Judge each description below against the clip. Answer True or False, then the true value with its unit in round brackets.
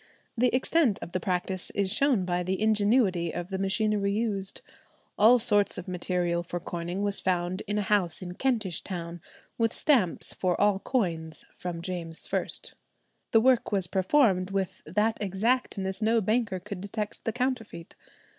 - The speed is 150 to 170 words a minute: True (160 wpm)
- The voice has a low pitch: False (195 Hz)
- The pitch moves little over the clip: False (3.6 semitones)